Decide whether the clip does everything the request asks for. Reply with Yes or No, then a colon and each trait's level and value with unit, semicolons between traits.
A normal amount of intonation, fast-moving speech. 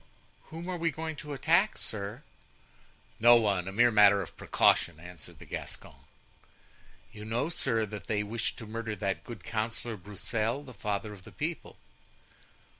No: average, 4.4 semitones; average, 160 wpm